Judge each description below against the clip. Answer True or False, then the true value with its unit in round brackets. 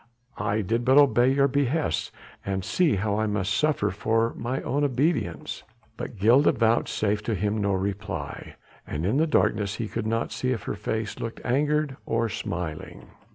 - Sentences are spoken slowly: False (160 wpm)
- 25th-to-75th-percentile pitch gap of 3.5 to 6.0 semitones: True (4.5 semitones)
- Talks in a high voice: False (115 Hz)